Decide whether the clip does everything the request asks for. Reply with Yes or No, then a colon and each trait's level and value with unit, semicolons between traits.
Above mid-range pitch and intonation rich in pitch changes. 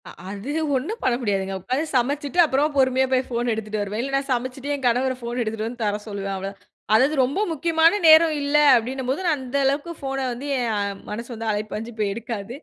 No: very high, 250 Hz; average, 4.3 semitones